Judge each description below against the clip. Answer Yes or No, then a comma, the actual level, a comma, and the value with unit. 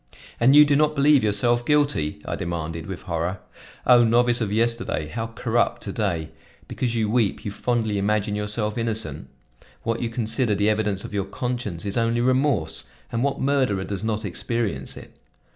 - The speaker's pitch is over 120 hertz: No, low, 110 Hz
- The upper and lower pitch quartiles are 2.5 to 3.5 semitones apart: Yes, average, 3.2 semitones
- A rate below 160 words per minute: No, average, 175 wpm